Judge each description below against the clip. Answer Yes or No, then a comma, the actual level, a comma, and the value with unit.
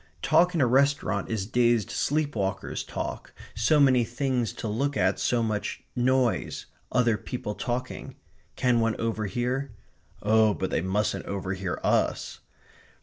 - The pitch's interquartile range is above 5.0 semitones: No, average, 3.6 semitones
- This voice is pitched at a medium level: No, low, 115 Hz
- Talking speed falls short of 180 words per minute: Yes, average, 140 wpm